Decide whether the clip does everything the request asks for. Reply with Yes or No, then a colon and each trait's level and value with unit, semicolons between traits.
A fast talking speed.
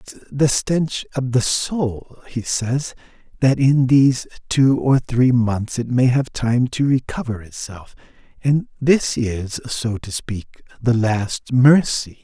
No: average, 150 wpm